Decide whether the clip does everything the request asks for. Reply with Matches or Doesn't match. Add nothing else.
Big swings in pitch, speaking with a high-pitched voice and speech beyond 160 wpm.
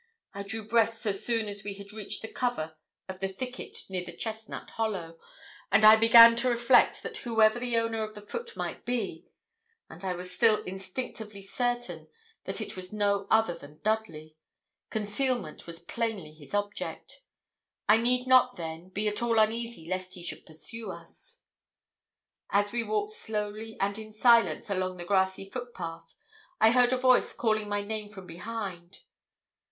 Doesn't match